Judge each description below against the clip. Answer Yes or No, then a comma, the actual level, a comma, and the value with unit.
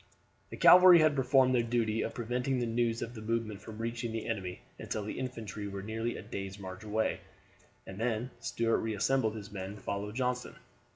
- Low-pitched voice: Yes, low, 115 Hz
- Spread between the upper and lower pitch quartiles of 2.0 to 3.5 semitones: Yes, average, 2.8 semitones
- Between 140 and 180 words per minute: No, average, 190 wpm